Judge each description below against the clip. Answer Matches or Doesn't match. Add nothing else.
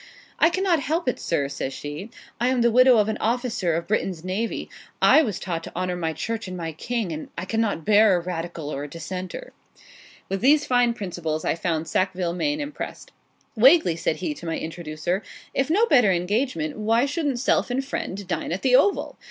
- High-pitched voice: Matches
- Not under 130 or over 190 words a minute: Doesn't match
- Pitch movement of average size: Doesn't match